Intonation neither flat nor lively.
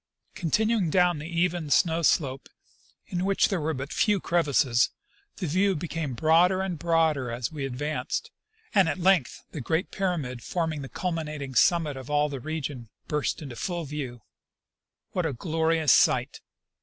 Yes: average, 3.9 semitones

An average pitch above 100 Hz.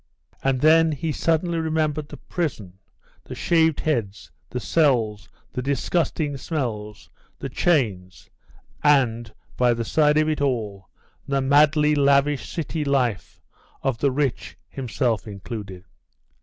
Yes: medium, 140 Hz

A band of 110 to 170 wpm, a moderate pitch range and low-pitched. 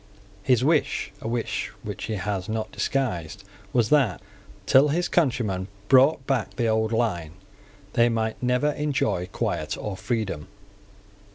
Yes: slow, 135 wpm; average, 4.5 semitones; low, 115 Hz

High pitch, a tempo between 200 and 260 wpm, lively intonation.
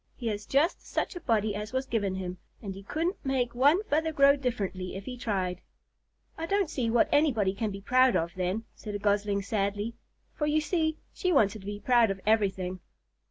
Yes: high, 220 Hz; fast, 205 wpm; wide, 5.8 semitones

